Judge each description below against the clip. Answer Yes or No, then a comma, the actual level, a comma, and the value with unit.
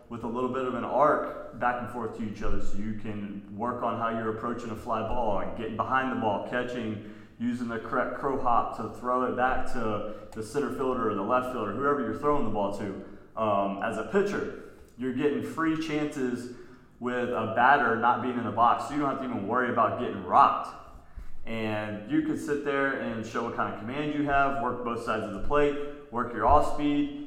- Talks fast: Yes, fast, 225 wpm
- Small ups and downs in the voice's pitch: No, average, 3.7 semitones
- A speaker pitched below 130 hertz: Yes, low, 120 Hz